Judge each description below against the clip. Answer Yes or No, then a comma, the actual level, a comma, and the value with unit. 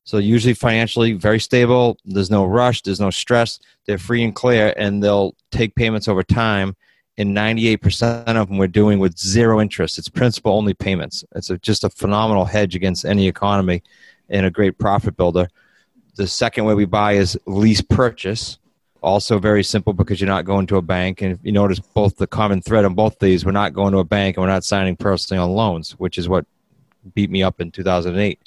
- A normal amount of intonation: No, narrow, 2.2 semitones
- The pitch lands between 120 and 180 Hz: No, low, 100 Hz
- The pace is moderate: No, fast, 210 wpm